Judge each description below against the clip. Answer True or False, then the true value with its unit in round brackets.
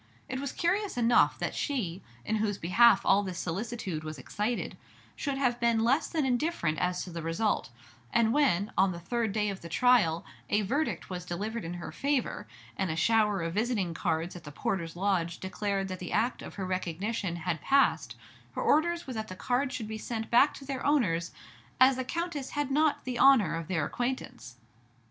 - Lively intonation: True (6.4 semitones)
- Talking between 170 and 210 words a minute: True (195 wpm)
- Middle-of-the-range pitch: False (215 Hz)